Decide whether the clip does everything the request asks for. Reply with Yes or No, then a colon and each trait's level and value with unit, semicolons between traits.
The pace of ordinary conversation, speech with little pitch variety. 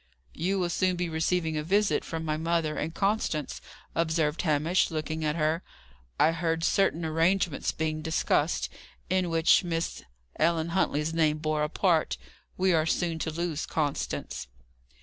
Yes: average, 150 wpm; narrow, 1.9 semitones